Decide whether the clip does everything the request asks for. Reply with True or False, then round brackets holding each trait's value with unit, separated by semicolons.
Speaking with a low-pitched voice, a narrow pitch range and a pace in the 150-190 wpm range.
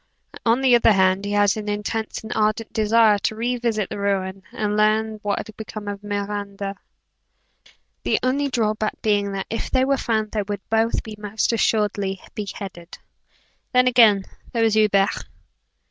False (215 Hz; 1.8 semitones; 170 wpm)